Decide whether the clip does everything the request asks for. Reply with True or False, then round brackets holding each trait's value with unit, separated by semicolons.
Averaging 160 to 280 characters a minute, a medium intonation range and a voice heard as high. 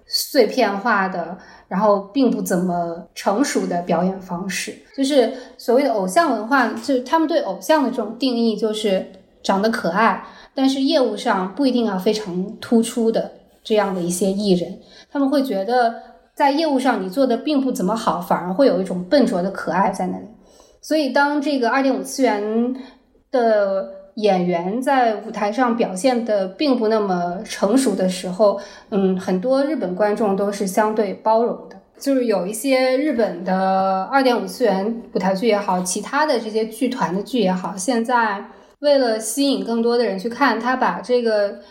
True (265 characters per minute; 4.5 semitones; 225 Hz)